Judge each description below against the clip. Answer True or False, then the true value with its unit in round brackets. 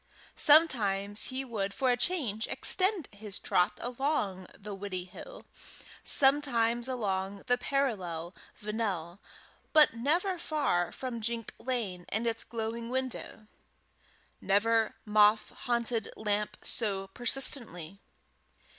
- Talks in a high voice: True (225 Hz)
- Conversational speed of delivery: False (105 wpm)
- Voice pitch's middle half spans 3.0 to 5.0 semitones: True (4.4 semitones)